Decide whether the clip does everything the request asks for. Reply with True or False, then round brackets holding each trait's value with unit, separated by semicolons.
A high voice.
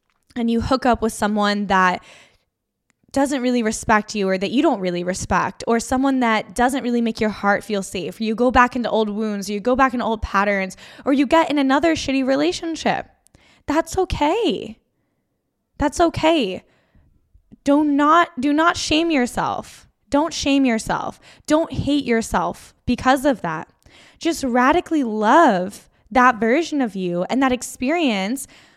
True (250 Hz)